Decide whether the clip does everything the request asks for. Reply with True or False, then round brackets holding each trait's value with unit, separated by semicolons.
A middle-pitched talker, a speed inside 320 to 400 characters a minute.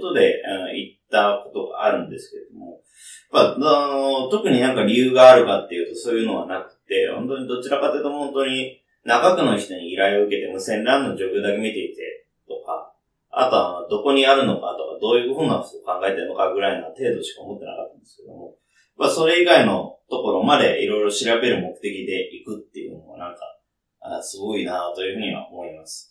False (165 Hz; 425 characters per minute)